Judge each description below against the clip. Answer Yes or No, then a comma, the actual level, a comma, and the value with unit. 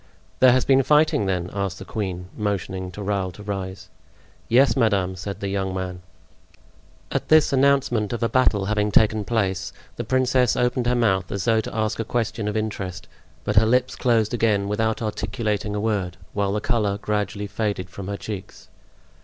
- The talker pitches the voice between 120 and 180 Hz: No, low, 105 Hz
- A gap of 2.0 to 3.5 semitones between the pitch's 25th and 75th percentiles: Yes, average, 3.0 semitones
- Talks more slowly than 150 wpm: No, average, 180 wpm